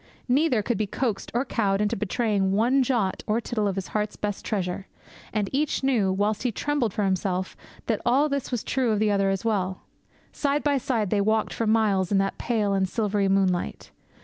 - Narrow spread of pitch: No, average, 3.5 semitones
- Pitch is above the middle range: Yes, high, 210 Hz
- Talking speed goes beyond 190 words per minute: Yes, average, 200 wpm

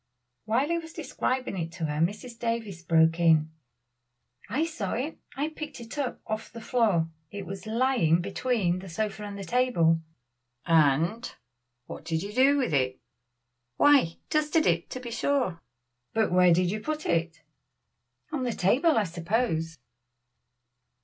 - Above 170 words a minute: No, average, 155 wpm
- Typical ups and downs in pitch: No, wide, 7.1 semitones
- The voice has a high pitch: Yes, high, 210 Hz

